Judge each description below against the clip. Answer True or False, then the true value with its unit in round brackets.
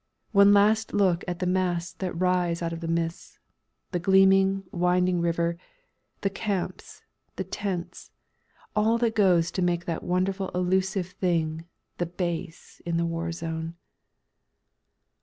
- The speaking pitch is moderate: True (180 Hz)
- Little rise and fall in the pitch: True (2.3 semitones)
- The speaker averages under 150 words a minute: True (140 wpm)